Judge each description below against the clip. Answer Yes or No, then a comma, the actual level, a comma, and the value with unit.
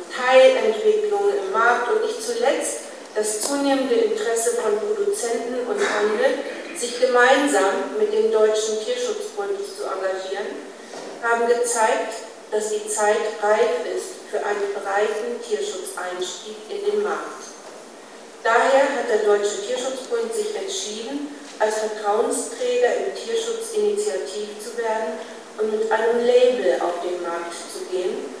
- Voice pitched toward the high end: Yes, very high, 255 Hz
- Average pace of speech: No, slow, 120 wpm